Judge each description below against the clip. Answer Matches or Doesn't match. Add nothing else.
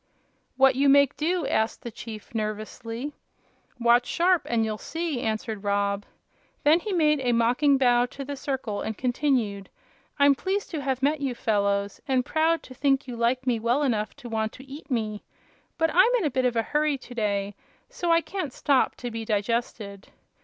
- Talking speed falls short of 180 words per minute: Doesn't match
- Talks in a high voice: Matches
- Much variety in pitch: Doesn't match